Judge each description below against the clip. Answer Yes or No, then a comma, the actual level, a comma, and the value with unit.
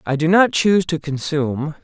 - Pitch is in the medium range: Yes, medium, 160 Hz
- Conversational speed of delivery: Yes, average, 195 wpm